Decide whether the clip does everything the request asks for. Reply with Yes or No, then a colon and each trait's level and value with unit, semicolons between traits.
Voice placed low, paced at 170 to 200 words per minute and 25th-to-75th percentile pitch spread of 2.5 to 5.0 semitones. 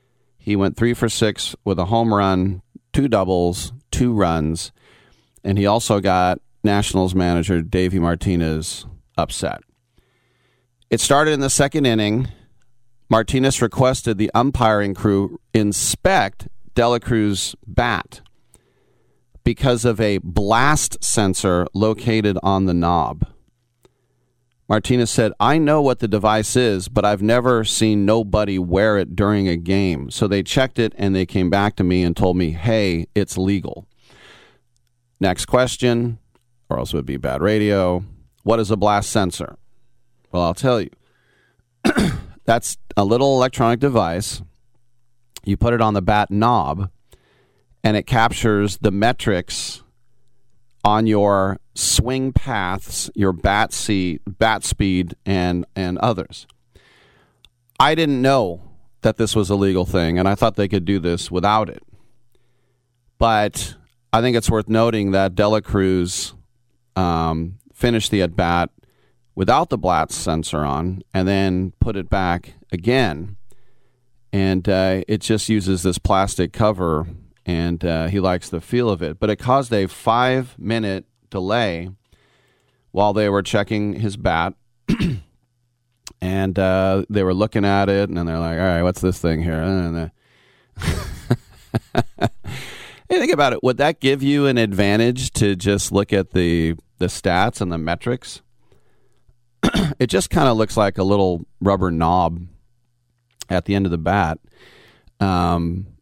No: low, 105 Hz; average, 145 wpm; average, 4.3 semitones